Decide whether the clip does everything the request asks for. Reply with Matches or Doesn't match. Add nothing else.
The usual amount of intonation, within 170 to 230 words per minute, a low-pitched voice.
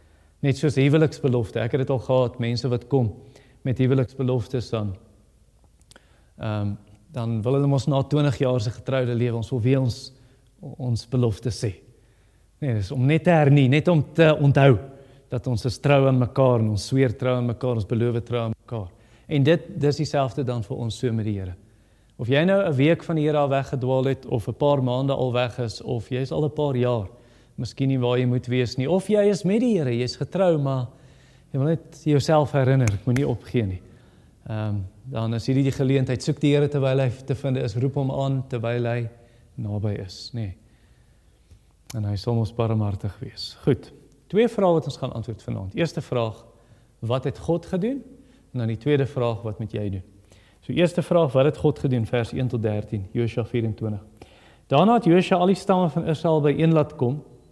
Matches